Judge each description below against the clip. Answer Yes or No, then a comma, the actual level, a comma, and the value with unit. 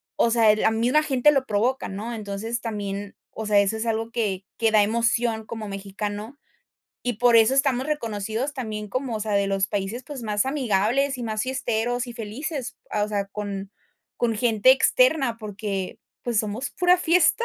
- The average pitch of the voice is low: No, high, 225 Hz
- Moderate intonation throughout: Yes, average, 3.4 semitones